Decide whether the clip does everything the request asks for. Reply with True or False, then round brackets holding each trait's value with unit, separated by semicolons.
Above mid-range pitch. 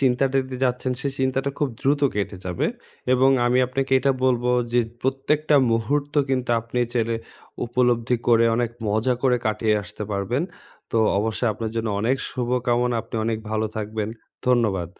False (125 Hz)